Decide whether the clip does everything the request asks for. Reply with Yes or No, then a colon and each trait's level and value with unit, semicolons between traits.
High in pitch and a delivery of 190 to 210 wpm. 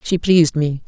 No: medium, 160 Hz; fast, 205 wpm